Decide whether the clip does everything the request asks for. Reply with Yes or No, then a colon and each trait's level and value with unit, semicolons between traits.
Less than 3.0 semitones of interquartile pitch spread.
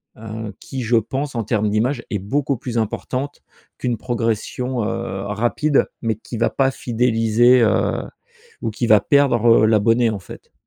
Yes: narrow, 2.6 semitones